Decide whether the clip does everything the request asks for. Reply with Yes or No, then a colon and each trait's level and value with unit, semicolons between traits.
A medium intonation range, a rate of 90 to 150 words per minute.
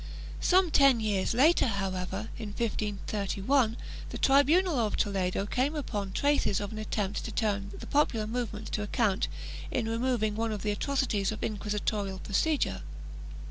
Yes: average, 4.2 semitones; average, 145 wpm